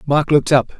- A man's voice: Yes, male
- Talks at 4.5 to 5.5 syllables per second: No, 6.2 syllables/s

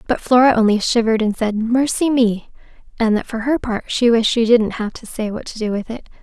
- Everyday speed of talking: No, fast, 240 wpm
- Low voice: No, high, 230 Hz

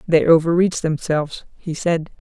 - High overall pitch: No, medium, 165 Hz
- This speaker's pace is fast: No, slow, 135 wpm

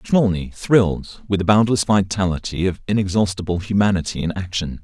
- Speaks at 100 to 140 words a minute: Yes, slow, 135 wpm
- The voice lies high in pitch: No, very low, 95 Hz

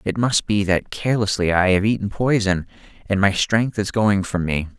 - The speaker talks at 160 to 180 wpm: No, average, 200 wpm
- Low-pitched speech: Yes, low, 100 Hz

